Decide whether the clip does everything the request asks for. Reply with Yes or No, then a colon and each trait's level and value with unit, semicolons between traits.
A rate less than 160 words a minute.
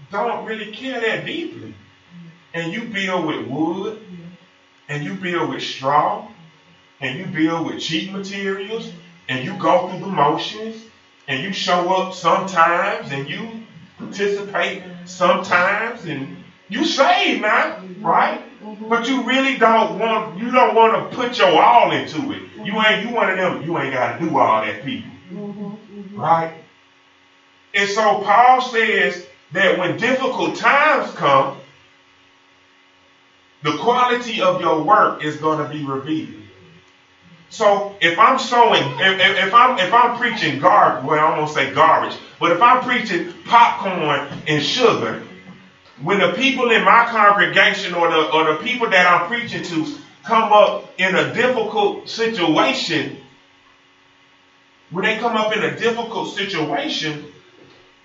Yes: average, 150 wpm